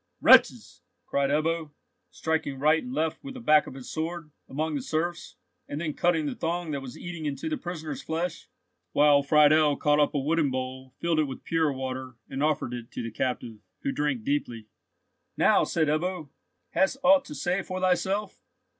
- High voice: No, medium, 155 Hz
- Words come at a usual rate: Yes, average, 185 wpm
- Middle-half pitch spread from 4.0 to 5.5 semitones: No, average, 3.6 semitones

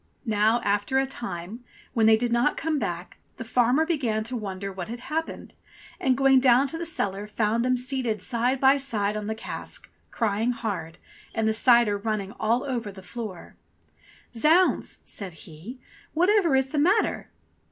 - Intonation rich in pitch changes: No, average, 4.3 semitones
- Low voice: No, high, 235 Hz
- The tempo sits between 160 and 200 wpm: Yes, average, 175 wpm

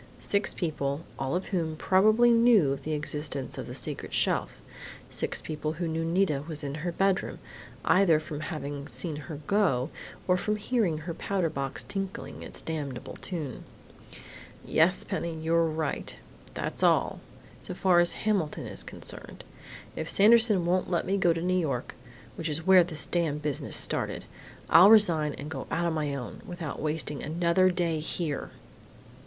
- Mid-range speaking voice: Yes, medium, 165 Hz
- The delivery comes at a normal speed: Yes, average, 160 wpm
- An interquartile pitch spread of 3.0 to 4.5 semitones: Yes, average, 3.5 semitones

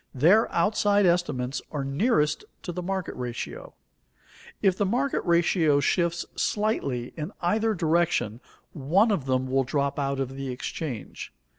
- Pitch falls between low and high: Yes, medium, 160 Hz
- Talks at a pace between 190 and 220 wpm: No, average, 140 wpm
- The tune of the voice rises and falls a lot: Yes, wide, 6.0 semitones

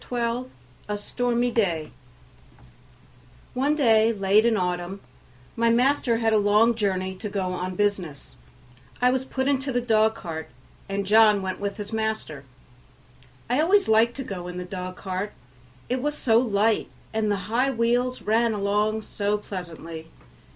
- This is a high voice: Yes, high, 215 Hz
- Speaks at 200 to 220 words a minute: No, average, 160 wpm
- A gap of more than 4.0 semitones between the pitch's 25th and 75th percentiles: No, average, 3.5 semitones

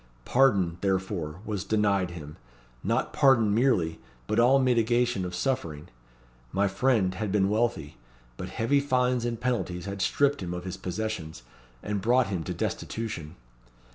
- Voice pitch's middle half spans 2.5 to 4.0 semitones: No, average, 5.0 semitones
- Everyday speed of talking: Yes, average, 145 wpm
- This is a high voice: No, low, 105 Hz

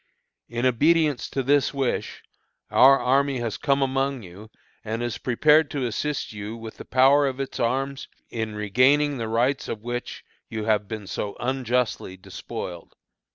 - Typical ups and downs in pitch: Yes, average, 3.7 semitones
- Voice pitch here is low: Yes, low, 125 Hz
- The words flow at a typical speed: Yes, average, 155 wpm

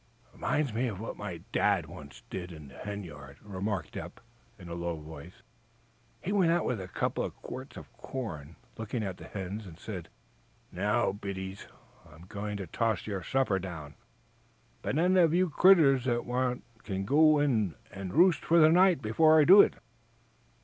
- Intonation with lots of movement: Yes, wide, 7.3 semitones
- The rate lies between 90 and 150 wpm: No, average, 180 wpm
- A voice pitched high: No, low, 105 Hz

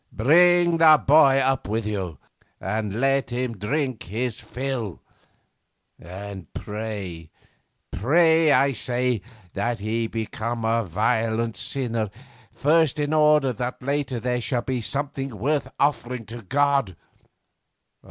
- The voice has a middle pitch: No, low, 120 Hz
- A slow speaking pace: Yes, slow, 120 wpm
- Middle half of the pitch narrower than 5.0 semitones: Yes, average, 4.2 semitones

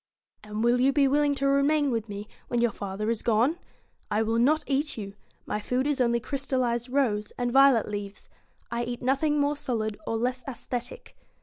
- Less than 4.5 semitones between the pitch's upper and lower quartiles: Yes, average, 3.8 semitones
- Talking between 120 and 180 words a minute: No, average, 195 wpm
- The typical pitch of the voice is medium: No, high, 245 Hz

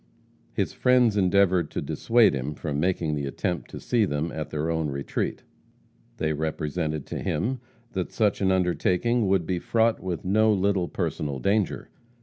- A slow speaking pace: No, average, 160 wpm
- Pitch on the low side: Yes, very low, 90 Hz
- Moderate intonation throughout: Yes, average, 4.9 semitones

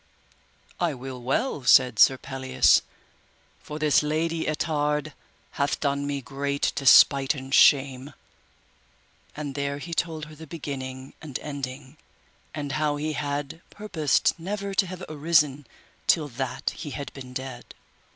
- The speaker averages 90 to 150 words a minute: Yes, slow, 135 wpm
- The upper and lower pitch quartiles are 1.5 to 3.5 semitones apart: Yes, narrow, 2.5 semitones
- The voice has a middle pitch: Yes, medium, 145 Hz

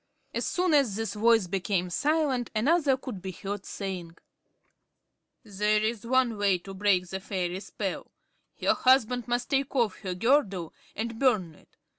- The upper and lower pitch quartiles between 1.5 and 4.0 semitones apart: No, average, 4.9 semitones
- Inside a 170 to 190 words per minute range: No, average, 155 wpm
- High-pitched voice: Yes, high, 215 Hz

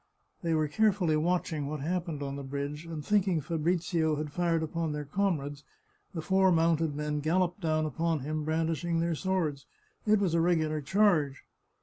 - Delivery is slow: No, average, 165 wpm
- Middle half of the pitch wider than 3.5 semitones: No, average, 2.7 semitones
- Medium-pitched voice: Yes, medium, 160 Hz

